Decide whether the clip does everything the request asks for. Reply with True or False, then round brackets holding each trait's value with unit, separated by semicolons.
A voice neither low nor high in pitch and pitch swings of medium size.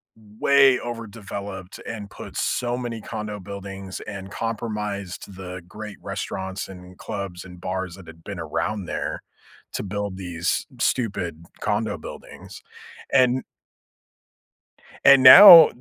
False (100 Hz; 3.4 semitones)